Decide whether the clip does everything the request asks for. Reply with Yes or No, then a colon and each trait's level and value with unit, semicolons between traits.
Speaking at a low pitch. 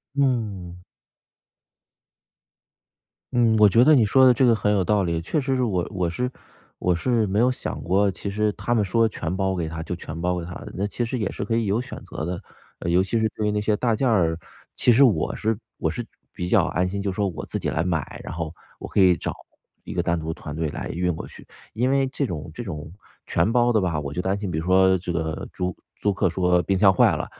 Yes: very low, 95 Hz